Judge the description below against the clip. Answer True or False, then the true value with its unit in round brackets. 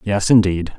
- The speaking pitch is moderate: False (100 Hz)